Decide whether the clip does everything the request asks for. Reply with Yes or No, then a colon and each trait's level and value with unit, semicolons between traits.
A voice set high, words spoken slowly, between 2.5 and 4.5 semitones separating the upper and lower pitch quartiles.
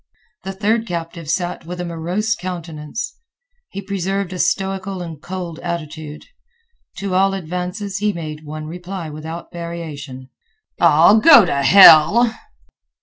No: medium, 175 Hz; slow, 130 wpm; average, 3.3 semitones